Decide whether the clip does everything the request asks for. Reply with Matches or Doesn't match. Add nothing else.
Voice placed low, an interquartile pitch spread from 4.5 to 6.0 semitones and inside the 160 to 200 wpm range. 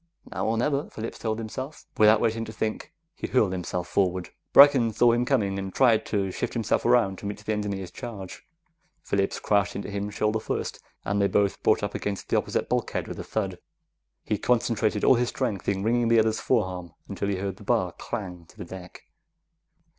Doesn't match